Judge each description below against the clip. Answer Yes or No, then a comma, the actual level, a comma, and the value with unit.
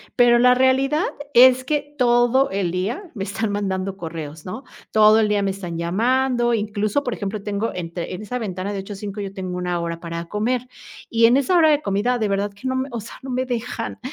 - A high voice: Yes, high, 215 Hz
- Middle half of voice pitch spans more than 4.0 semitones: Yes, average, 4.5 semitones